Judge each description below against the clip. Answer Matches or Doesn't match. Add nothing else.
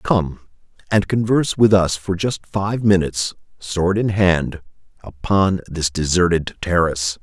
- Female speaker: Doesn't match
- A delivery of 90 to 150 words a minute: Matches